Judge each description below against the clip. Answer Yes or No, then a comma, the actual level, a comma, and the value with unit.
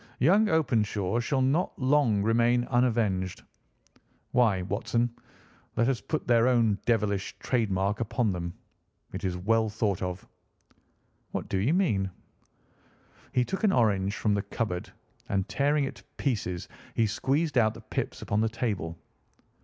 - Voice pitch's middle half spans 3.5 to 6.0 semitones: Yes, average, 4.1 semitones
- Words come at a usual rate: Yes, average, 145 wpm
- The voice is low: Yes, low, 115 Hz